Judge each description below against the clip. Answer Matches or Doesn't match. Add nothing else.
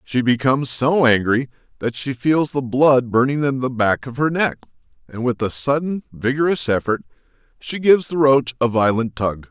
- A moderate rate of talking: Matches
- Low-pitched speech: Matches